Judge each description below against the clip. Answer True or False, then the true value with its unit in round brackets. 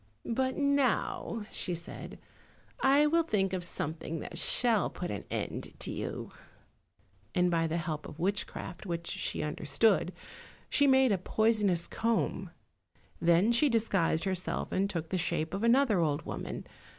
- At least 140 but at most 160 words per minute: True (150 wpm)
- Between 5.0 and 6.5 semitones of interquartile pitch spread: True (5.6 semitones)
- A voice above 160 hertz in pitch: True (190 Hz)